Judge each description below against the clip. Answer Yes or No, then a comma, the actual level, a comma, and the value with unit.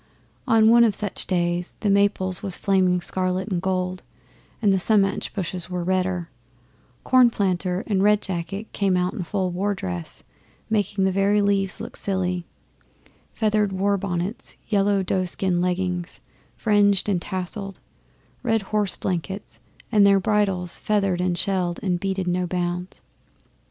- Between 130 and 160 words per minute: Yes, average, 140 wpm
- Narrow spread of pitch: Yes, narrow, 2.1 semitones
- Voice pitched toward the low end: No, high, 190 Hz